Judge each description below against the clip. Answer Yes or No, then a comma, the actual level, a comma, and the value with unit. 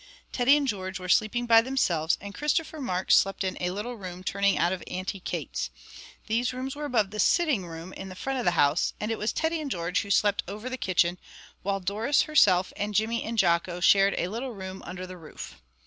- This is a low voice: No, high, 200 Hz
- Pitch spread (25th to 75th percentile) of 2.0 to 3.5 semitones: No, average, 4.8 semitones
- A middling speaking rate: No, fast, 220 wpm